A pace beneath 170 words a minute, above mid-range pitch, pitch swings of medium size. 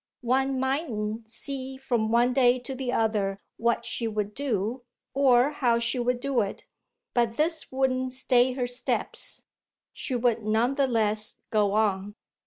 Yes: average, 155 wpm; high, 245 Hz; average, 3.1 semitones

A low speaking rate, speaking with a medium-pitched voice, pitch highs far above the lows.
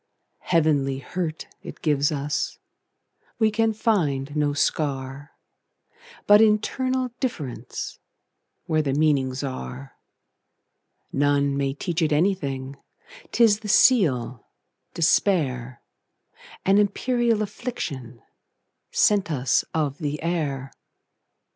Yes: slow, 80 wpm; medium, 150 Hz; wide, 7.1 semitones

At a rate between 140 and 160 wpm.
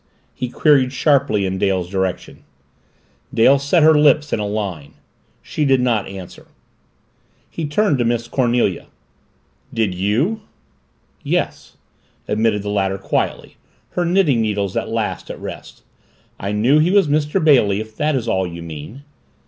Yes: average, 150 wpm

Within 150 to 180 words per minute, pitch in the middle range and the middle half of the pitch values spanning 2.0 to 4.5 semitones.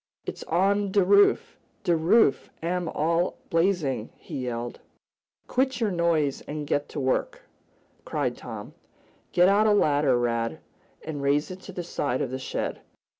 No: average, 155 wpm; medium, 165 Hz; average, 5.3 semitones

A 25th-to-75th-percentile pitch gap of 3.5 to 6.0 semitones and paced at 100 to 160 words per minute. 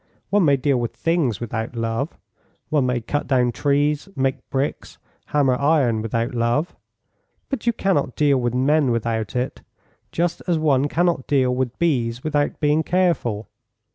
Yes: average, 4.2 semitones; average, 155 wpm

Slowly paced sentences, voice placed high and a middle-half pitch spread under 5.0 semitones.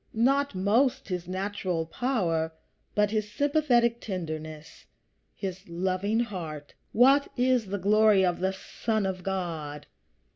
Yes: slow, 120 wpm; high, 195 Hz; average, 4.4 semitones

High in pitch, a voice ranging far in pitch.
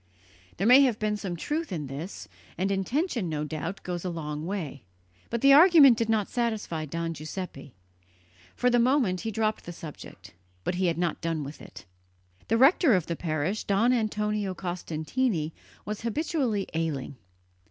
Yes: high, 195 Hz; wide, 6.1 semitones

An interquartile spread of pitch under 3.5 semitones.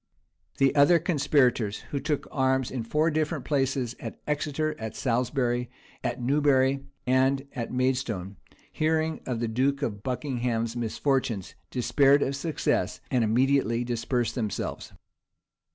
Yes: average, 2.9 semitones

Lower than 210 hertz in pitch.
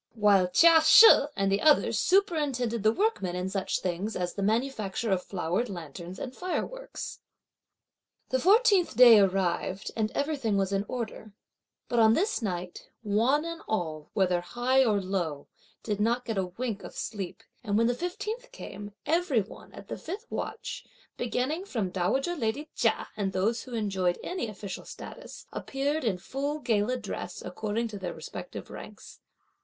No: high, 220 Hz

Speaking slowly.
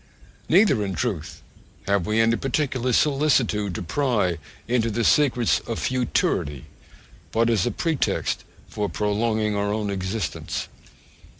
Yes: slow, 125 wpm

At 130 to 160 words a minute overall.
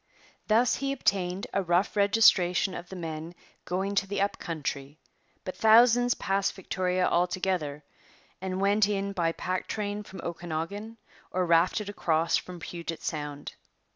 Yes: average, 140 wpm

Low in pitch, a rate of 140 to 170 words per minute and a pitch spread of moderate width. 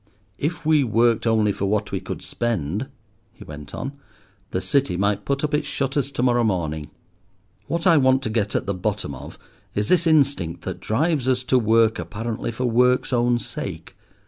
No: low, 120 Hz; average, 185 wpm; average, 4.7 semitones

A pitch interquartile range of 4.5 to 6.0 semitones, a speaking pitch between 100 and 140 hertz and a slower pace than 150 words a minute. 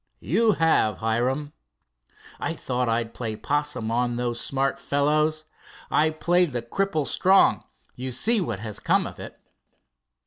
Yes: average, 4.9 semitones; low, 135 Hz; average, 140 wpm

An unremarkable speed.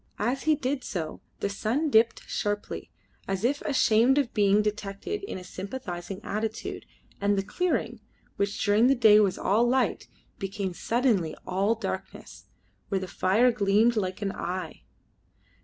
Yes: average, 150 wpm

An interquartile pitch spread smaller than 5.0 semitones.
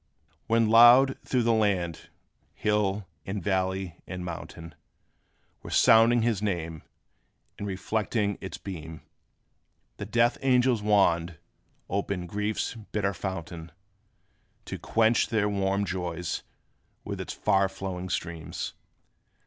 Yes: average, 3.6 semitones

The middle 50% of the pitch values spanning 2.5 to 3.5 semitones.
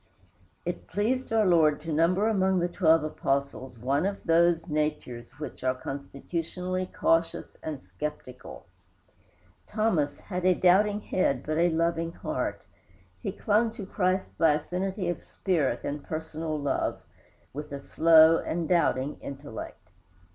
No: average, 4.0 semitones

